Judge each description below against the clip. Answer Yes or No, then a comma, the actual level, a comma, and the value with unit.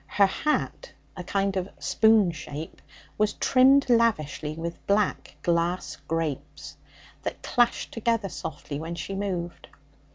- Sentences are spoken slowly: Yes, slow, 125 wpm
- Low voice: No, high, 190 Hz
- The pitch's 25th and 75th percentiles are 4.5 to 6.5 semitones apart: Yes, average, 5.2 semitones